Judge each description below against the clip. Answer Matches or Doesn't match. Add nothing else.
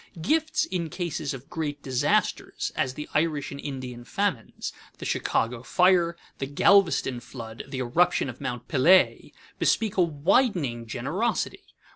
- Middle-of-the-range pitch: Matches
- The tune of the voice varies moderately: Doesn't match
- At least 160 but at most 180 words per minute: Doesn't match